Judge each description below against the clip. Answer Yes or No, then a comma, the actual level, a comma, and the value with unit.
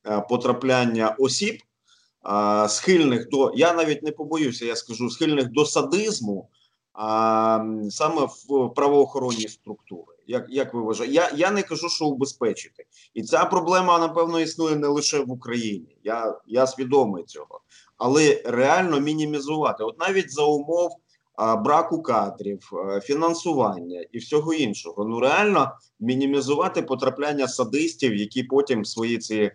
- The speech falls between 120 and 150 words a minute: Yes, average, 125 wpm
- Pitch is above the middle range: No, low, 135 Hz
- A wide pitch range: Yes, wide, 6.5 semitones